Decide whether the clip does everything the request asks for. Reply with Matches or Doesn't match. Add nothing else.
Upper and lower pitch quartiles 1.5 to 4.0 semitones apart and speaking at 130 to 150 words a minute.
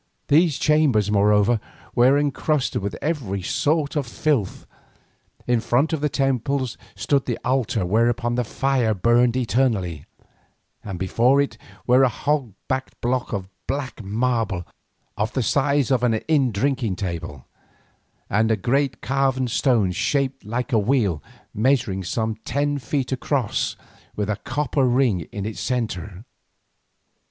Doesn't match